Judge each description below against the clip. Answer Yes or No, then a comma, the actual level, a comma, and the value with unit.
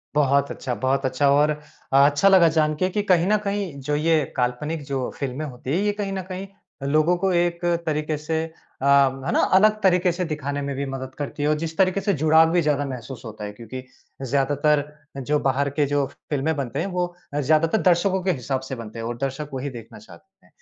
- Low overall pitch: No, medium, 150 Hz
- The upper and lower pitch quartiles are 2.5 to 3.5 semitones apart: No, average, 4.2 semitones